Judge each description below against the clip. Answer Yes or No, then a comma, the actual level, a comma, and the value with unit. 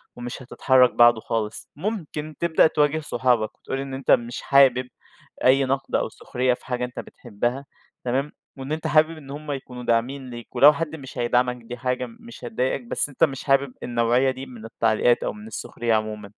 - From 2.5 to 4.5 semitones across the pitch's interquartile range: Yes, average, 3.1 semitones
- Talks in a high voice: No, low, 130 Hz